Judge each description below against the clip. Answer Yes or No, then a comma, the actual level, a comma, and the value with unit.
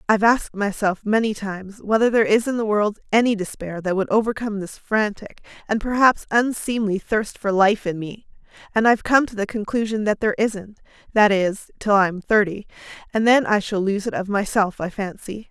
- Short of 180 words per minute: No, average, 195 wpm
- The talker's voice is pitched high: Yes, high, 210 Hz